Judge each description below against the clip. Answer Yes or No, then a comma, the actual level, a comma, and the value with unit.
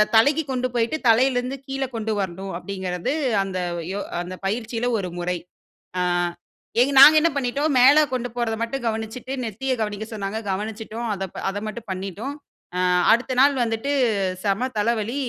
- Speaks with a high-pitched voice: Yes, high, 225 Hz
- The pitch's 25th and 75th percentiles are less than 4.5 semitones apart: Yes, average, 4.1 semitones